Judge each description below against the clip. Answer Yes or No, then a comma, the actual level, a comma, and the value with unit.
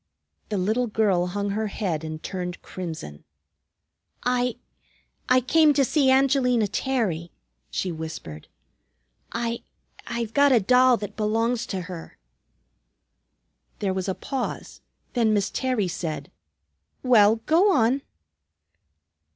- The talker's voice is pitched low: No, high, 220 Hz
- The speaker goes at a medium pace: No, slow, 120 wpm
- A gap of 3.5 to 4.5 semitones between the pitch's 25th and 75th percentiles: No, average, 5.3 semitones